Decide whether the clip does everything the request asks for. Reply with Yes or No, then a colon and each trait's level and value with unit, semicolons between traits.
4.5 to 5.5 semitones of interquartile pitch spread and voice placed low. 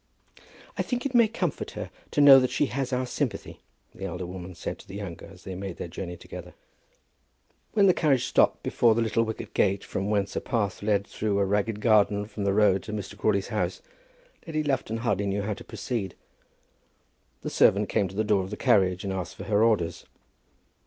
No: average, 3.0 semitones; low, 105 Hz